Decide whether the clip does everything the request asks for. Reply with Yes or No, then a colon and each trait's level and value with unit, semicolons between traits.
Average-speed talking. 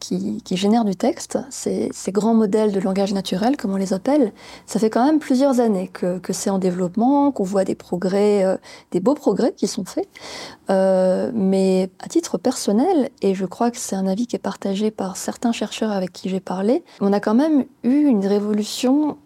Yes: average, 210 wpm